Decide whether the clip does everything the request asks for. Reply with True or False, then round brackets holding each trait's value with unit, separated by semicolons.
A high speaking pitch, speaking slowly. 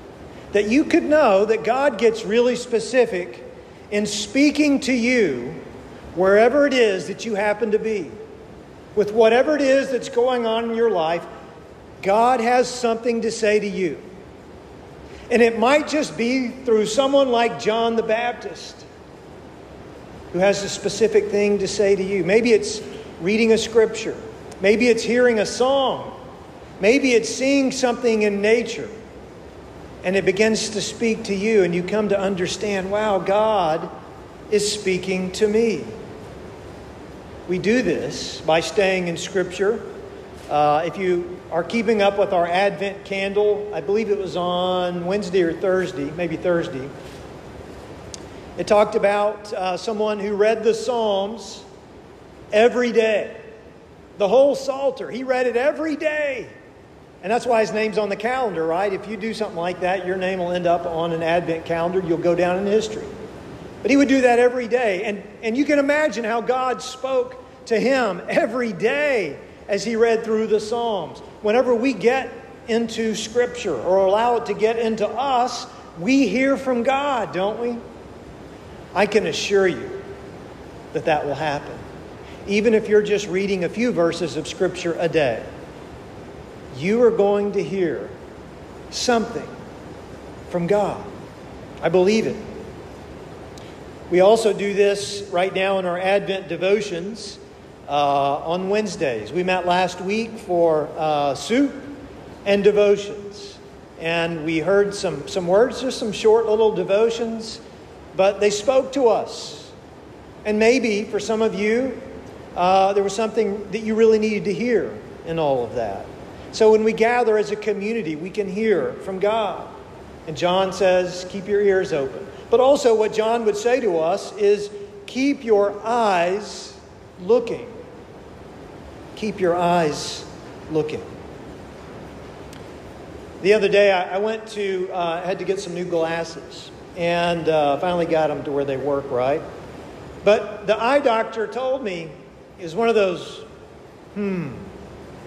False (210 Hz; 155 wpm)